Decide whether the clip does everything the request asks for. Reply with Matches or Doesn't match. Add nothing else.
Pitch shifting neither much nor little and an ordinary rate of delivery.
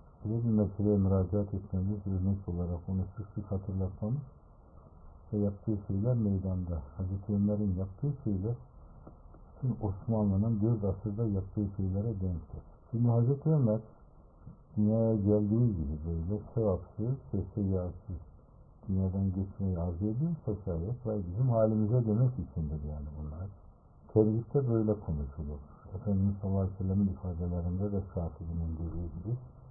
Matches